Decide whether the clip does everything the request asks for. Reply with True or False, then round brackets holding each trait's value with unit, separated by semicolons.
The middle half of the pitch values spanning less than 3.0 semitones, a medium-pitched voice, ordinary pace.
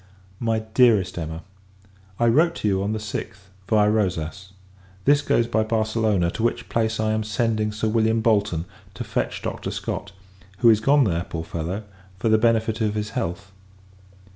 False (2.5 semitones; 110 Hz; 170 wpm)